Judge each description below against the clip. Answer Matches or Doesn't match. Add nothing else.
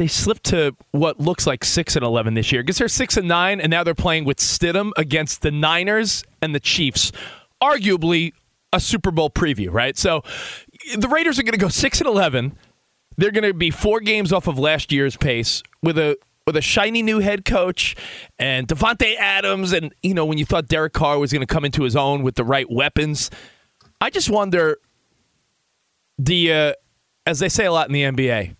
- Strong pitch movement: Matches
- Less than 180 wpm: Doesn't match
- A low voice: Doesn't match